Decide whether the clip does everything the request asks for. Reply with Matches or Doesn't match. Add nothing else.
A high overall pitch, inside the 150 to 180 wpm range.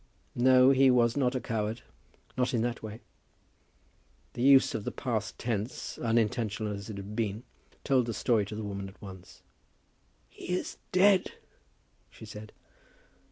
Doesn't match